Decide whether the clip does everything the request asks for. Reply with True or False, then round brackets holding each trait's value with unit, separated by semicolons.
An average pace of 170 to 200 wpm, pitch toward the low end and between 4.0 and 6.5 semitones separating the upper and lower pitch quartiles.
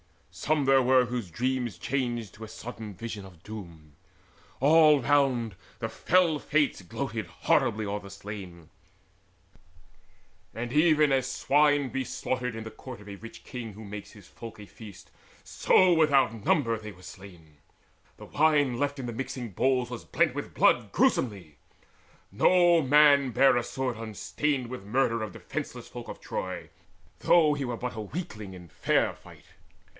False (160 wpm; 120 Hz; 5.0 semitones)